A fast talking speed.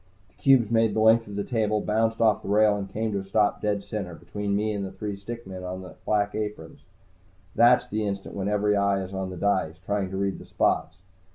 Yes: fast, 240 wpm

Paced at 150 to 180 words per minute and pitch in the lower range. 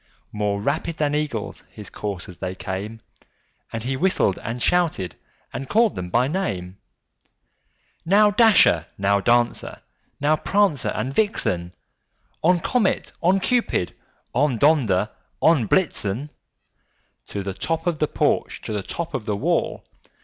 No: slow, 135 wpm; low, 125 Hz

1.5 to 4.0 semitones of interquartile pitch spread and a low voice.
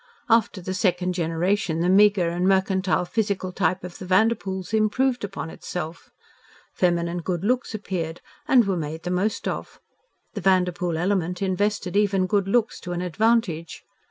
No: narrow, 2.6 semitones; medium, 185 Hz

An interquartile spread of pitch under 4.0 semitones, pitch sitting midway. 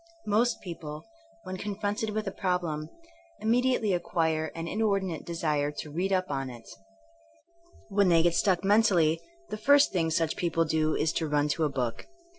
No: average, 4.5 semitones; medium, 170 Hz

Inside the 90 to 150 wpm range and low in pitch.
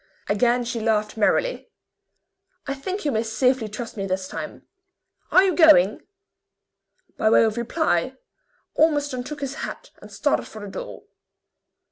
No: average, 145 wpm; high, 240 Hz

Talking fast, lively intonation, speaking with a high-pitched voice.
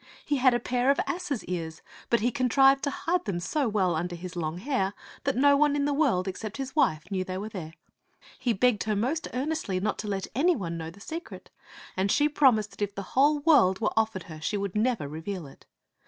Yes: fast, 230 wpm; wide, 7.0 semitones; high, 220 Hz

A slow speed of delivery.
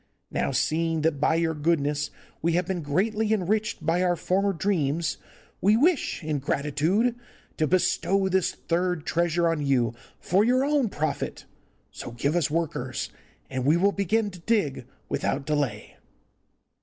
No: average, 150 wpm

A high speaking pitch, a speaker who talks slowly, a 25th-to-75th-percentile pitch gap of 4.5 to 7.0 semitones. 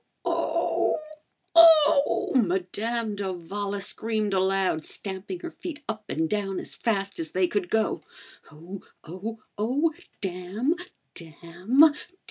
No: high, 205 Hz; slow, 110 wpm; average, 4.0 semitones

